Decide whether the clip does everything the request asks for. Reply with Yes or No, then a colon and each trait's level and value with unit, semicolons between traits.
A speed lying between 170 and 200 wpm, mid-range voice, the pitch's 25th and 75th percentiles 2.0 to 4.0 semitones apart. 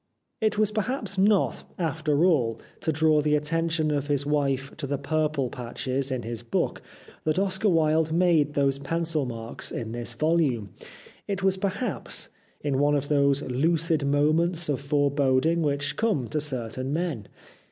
No: average, 160 wpm; medium, 150 Hz; average, 3.3 semitones